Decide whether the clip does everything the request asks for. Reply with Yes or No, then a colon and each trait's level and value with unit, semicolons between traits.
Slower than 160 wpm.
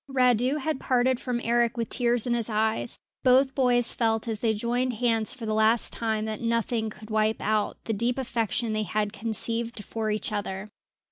No: average, 190 wpm